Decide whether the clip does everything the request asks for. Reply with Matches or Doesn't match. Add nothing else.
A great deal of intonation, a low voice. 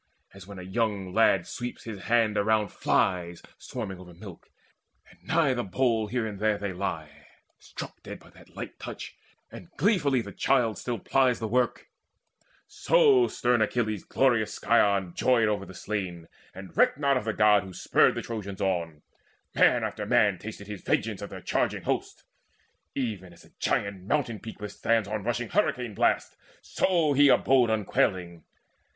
Doesn't match